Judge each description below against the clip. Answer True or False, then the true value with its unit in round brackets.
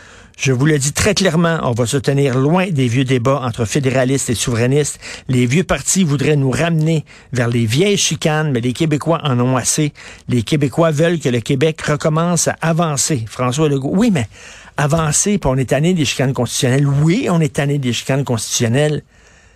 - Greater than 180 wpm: True (190 wpm)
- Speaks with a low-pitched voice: False (145 Hz)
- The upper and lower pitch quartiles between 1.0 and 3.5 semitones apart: False (4.2 semitones)